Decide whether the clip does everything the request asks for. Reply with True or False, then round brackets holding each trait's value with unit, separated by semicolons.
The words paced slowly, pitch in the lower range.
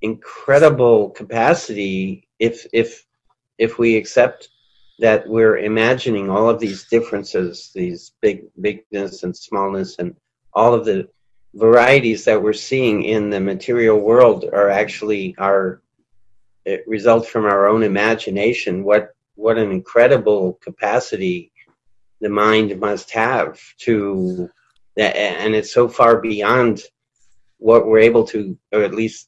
True (125 wpm; 105 Hz)